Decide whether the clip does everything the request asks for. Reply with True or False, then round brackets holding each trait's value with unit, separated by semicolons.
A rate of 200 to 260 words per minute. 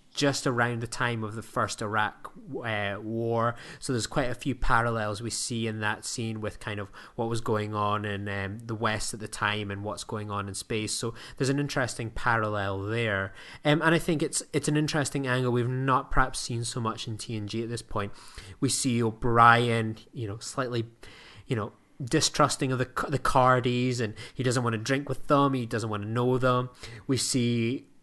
True (205 wpm)